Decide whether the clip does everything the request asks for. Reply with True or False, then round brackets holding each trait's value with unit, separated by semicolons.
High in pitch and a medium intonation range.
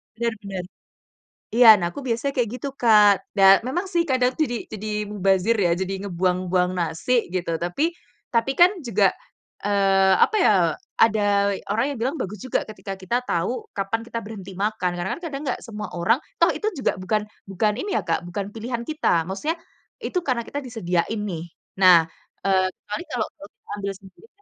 True (210 Hz; 4.0 semitones)